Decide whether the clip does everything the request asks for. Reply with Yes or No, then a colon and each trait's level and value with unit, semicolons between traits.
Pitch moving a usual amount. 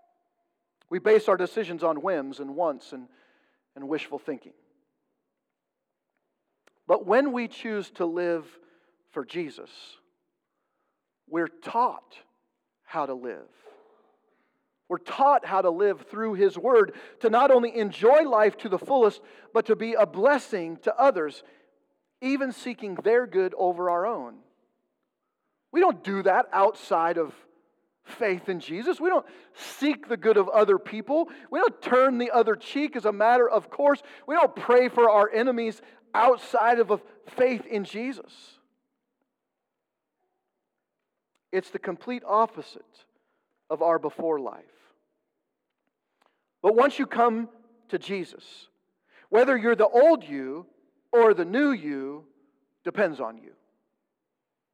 No: wide, 6.7 semitones